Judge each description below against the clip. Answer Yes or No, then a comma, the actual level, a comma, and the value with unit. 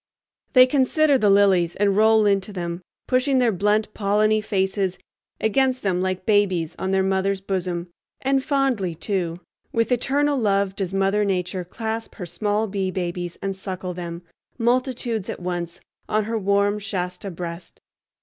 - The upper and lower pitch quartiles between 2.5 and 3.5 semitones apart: Yes, average, 3.2 semitones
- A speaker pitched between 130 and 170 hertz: No, high, 200 Hz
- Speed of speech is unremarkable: Yes, average, 150 wpm